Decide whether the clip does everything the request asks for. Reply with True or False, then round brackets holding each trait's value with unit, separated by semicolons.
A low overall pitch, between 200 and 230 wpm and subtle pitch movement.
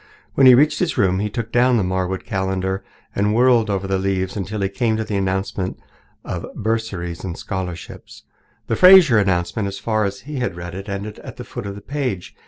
False (100 Hz; 205 wpm; 3.3 semitones)